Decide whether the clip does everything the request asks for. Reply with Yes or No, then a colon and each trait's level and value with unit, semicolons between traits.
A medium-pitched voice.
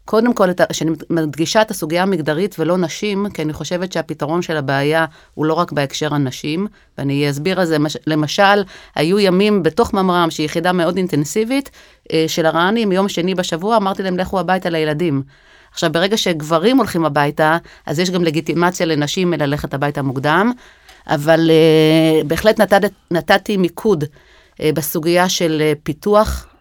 Yes: medium, 170 Hz